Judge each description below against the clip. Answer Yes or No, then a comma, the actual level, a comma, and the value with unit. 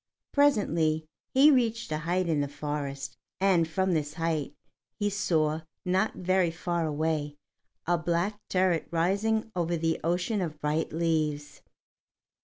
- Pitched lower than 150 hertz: No, medium, 165 Hz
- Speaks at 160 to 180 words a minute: No, slow, 135 wpm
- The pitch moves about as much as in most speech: Yes, average, 3.4 semitones